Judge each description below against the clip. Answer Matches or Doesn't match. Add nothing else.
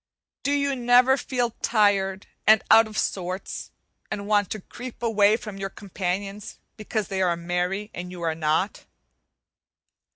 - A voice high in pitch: Matches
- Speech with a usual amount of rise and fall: Matches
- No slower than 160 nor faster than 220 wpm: Doesn't match